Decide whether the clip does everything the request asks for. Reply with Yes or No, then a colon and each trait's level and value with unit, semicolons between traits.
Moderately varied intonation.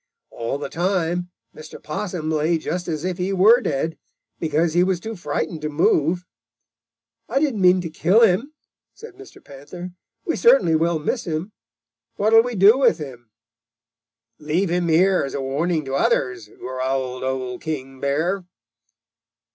Yes: average, 4.4 semitones